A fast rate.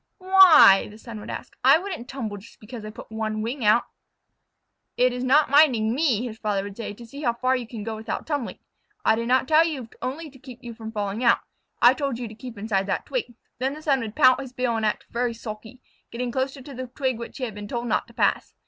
Yes: fast, 245 wpm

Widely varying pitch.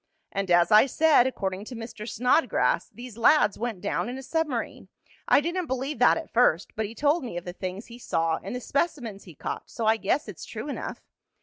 No: average, 4.9 semitones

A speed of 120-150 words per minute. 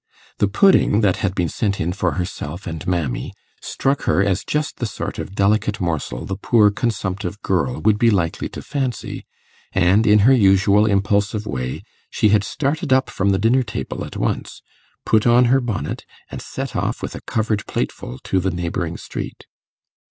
No: average, 180 wpm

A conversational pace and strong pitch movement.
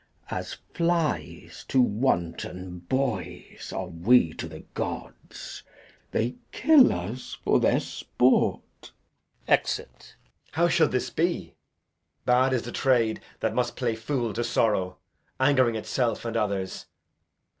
No: slow, 125 wpm; wide, 5.7 semitones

